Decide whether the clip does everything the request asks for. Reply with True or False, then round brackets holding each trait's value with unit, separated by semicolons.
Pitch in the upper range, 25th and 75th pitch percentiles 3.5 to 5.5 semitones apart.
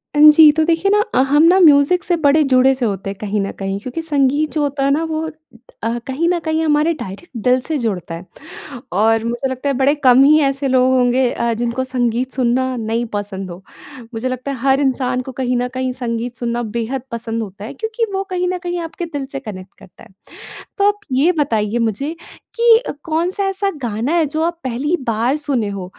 True (260 Hz; 5.1 semitones)